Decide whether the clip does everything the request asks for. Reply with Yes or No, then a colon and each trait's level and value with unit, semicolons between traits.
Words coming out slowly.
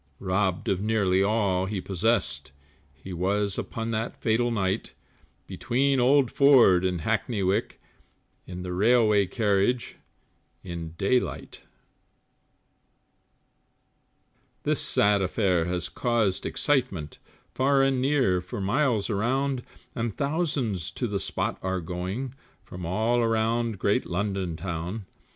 Yes: slow, 120 wpm